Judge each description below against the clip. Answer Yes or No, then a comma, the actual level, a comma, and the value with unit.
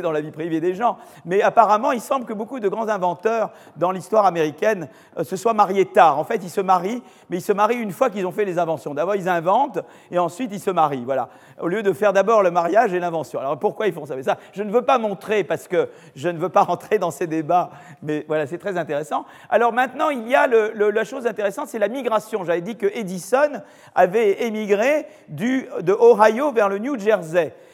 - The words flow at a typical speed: No, fast, 235 wpm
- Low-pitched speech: No, high, 205 Hz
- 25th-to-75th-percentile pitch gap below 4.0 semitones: No, average, 4.6 semitones